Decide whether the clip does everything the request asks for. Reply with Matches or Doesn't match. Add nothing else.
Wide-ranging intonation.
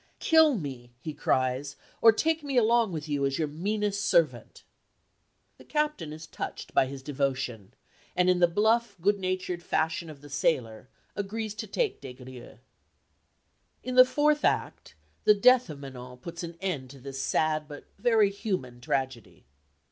Matches